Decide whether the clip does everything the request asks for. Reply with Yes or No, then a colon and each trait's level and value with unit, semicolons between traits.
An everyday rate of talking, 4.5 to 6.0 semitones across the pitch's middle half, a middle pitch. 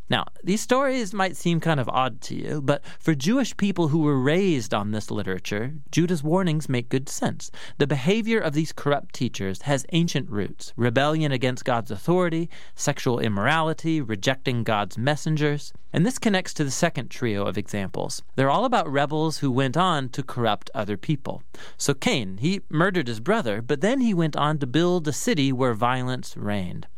Yes: average, 180 wpm; average, 5.3 semitones; medium, 145 Hz